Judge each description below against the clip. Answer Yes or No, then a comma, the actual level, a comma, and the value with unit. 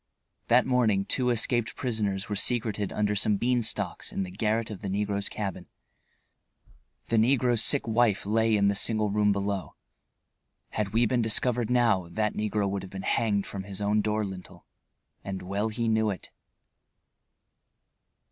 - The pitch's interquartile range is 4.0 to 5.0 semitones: No, narrow, 2.5 semitones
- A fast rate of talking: No, average, 160 wpm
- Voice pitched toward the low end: Yes, low, 105 Hz